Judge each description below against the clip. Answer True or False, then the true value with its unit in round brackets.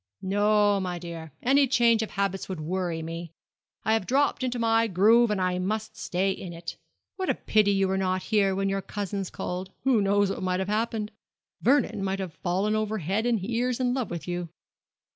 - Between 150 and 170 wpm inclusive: False (200 wpm)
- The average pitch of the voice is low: False (200 Hz)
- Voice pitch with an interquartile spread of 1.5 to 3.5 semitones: True (3.2 semitones)